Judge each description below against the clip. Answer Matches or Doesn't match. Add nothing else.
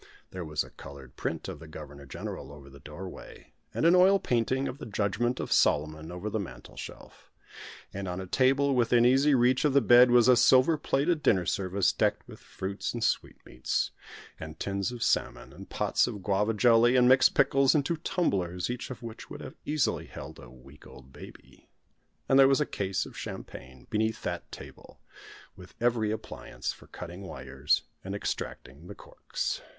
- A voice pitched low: Matches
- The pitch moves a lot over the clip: Matches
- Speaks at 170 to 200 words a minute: Matches